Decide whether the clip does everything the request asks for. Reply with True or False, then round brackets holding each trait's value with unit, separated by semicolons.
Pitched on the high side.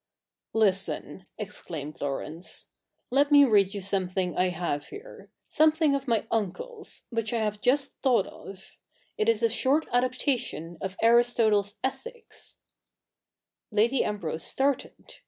True (220 Hz)